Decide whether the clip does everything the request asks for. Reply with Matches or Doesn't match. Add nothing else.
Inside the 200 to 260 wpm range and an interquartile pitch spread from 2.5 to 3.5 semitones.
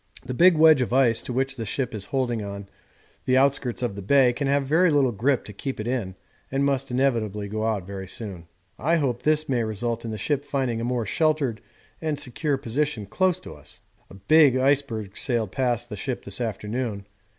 Doesn't match